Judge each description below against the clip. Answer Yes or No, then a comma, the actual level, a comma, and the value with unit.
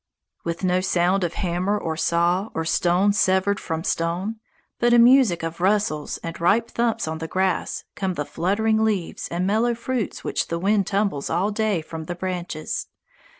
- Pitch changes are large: No, average, 3.7 semitones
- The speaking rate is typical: Yes, average, 175 wpm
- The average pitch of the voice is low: No, medium, 185 Hz